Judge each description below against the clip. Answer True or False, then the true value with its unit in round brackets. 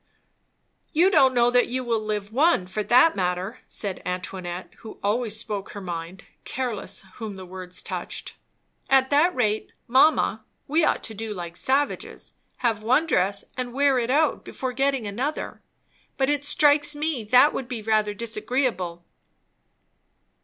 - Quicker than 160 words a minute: False (155 wpm)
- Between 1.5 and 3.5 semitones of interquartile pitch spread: False (5.1 semitones)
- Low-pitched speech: False (235 Hz)